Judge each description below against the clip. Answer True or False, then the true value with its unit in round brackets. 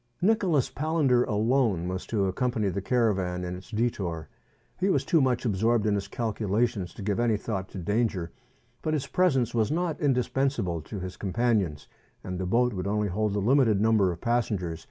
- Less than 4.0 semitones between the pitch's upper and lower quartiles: False (4.7 semitones)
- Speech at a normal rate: True (180 wpm)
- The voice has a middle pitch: False (110 Hz)